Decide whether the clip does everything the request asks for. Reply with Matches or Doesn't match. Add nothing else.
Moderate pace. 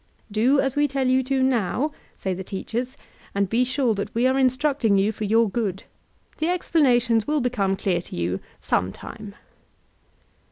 Matches